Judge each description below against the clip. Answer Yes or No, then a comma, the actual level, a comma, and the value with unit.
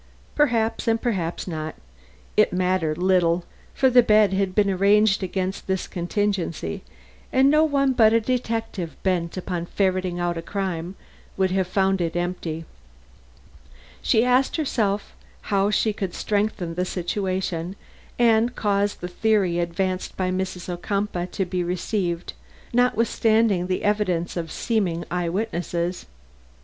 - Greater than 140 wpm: No, slow, 135 wpm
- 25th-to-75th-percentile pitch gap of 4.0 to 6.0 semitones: No, average, 3.5 semitones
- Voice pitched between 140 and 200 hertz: Yes, high, 190 Hz